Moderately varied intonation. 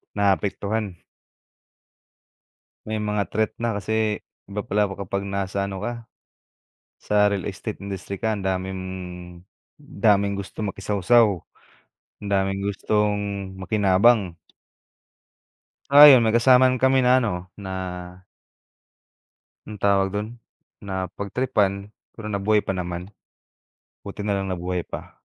No: narrow, 2.0 semitones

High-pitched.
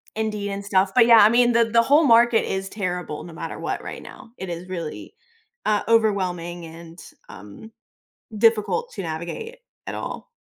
Yes: high, 200 Hz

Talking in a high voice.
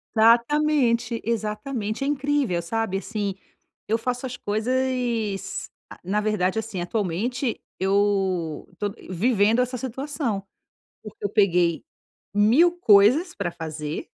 Yes: high, 215 Hz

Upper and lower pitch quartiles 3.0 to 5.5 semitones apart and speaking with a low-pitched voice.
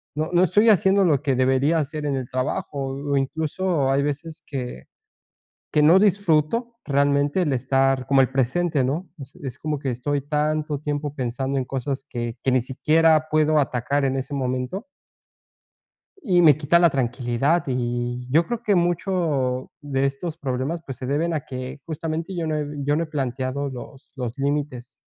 No: average, 3.3 semitones; medium, 145 Hz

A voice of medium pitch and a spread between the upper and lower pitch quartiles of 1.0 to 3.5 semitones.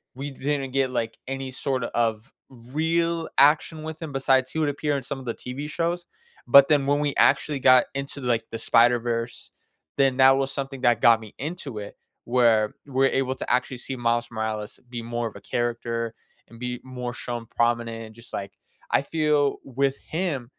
No: low, 130 Hz; average, 2.9 semitones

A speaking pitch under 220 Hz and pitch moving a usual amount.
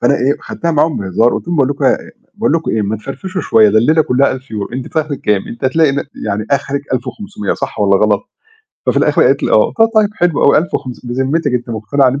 No: low, 135 Hz; wide, 5.8 semitones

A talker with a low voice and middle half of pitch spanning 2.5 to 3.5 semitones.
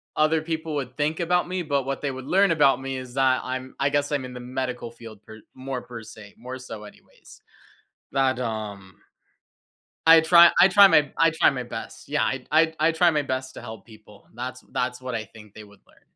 No: low, 130 Hz; average, 4.3 semitones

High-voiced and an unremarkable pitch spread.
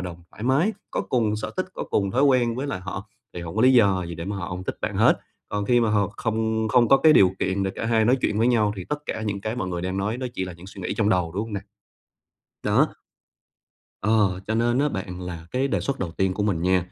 No: low, 105 Hz; average, 4.1 semitones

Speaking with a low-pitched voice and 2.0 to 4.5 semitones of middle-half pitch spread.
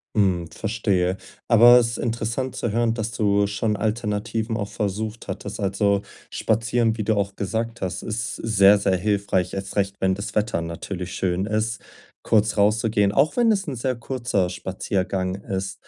Yes: low, 105 Hz; narrow, 2.6 semitones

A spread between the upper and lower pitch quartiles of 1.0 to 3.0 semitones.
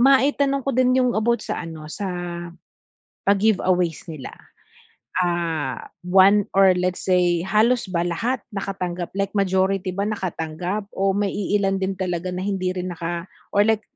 Yes: average, 2.7 semitones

